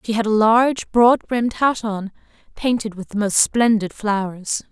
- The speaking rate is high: No, average, 180 wpm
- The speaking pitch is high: Yes, high, 220 Hz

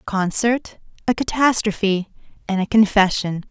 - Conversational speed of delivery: No, slow, 120 wpm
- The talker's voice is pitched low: No, high, 210 Hz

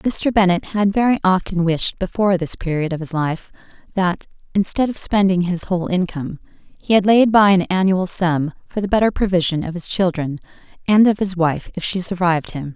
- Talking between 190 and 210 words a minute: Yes, average, 195 wpm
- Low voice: No, medium, 185 Hz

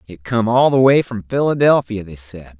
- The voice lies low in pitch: Yes, low, 115 Hz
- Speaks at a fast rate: Yes, fast, 210 wpm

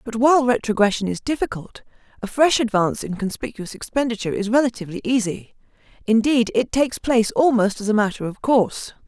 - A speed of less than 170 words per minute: Yes, average, 160 wpm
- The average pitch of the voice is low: No, high, 230 Hz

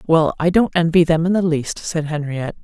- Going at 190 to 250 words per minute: Yes, fast, 205 wpm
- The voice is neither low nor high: Yes, medium, 165 Hz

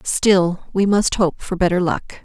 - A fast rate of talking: No, average, 190 wpm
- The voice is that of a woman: Yes, female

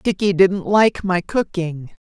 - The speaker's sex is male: No, female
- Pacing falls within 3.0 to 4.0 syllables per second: Yes, 3.6 syllables/s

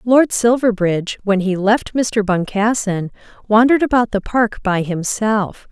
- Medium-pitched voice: No, high, 210 Hz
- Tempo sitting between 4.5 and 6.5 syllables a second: No, 4.3 syllables/s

